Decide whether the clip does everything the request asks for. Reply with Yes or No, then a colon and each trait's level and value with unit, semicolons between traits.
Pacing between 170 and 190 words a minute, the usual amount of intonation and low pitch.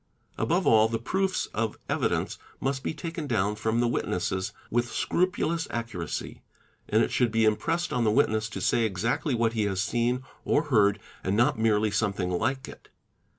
Yes: average, 175 wpm; average, 3.6 semitones; low, 115 Hz